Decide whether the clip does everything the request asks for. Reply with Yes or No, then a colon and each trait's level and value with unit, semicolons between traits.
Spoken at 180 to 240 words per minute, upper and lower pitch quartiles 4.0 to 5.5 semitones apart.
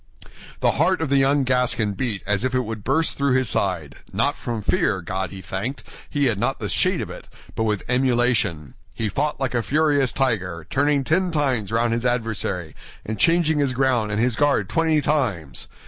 Yes: average, 195 wpm; average, 5.0 semitones